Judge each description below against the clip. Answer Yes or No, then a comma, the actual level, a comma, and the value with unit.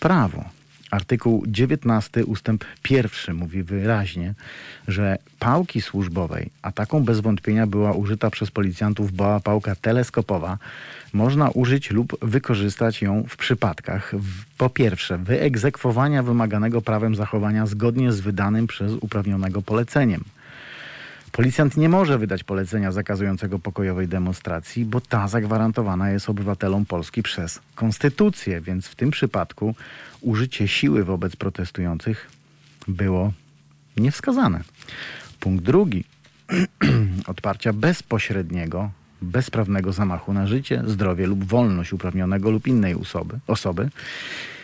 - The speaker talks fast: No, slow, 110 wpm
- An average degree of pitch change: Yes, average, 3.7 semitones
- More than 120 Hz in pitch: No, low, 110 Hz